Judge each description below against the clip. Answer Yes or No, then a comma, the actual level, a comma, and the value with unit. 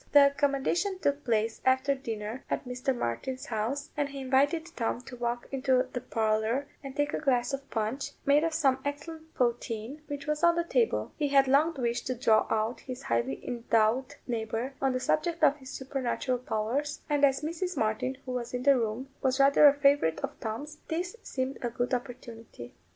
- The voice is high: Yes, very high, 265 Hz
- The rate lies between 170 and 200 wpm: Yes, average, 190 wpm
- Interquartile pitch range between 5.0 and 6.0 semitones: No, average, 3.2 semitones